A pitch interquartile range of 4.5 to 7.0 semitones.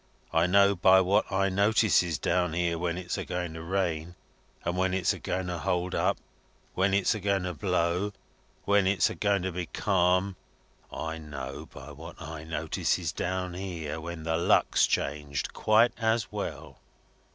No: average, 2.7 semitones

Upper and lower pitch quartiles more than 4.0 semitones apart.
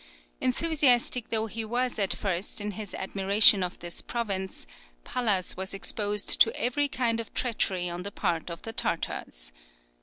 No: average, 3.7 semitones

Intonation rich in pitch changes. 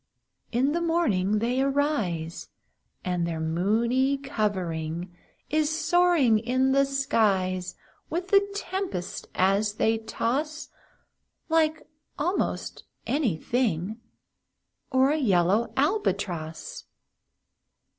Yes: wide, 8.1 semitones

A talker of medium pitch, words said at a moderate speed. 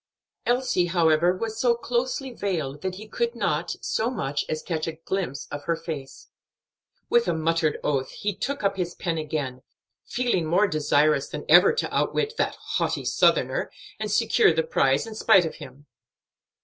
Yes: medium, 175 Hz; average, 170 wpm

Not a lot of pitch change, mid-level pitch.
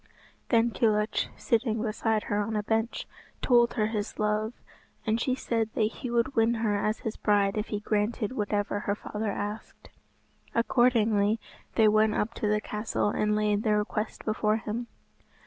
No: narrow, 1.4 semitones; high, 215 Hz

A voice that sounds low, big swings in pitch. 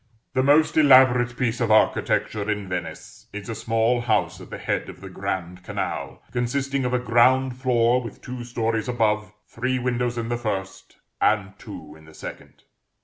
No: low, 120 Hz; average, 3.0 semitones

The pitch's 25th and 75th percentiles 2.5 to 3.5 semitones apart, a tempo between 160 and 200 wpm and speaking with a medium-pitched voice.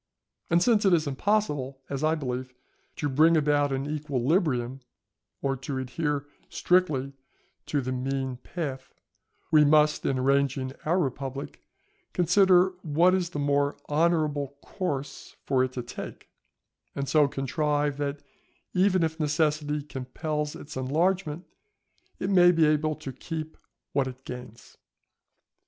No: average, 3.2 semitones; slow, 135 wpm; medium, 145 Hz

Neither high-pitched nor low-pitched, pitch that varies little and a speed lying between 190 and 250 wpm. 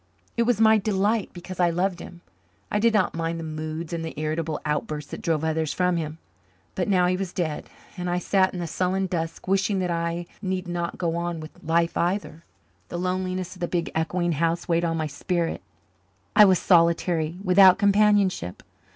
Yes: medium, 175 Hz; narrow, 2.3 semitones; average, 195 wpm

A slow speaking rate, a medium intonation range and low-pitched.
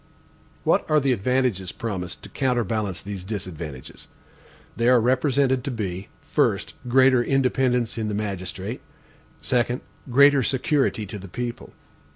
Yes: slow, 130 wpm; average, 4.7 semitones; low, 120 Hz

